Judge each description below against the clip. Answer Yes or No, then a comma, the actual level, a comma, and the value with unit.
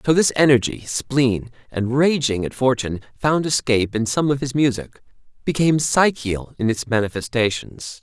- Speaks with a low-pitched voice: Yes, low, 130 Hz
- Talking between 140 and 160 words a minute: Yes, average, 150 wpm